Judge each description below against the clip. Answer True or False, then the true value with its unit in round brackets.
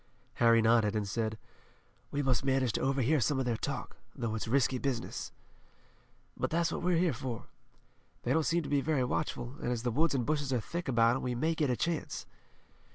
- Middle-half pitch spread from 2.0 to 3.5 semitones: False (4.1 semitones)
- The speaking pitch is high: False (130 Hz)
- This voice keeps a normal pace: False (210 wpm)